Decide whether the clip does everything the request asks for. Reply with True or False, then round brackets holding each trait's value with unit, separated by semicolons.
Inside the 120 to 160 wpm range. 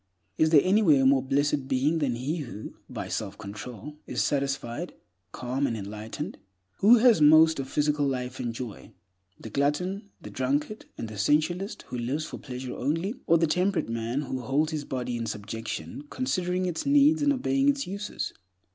False (175 wpm)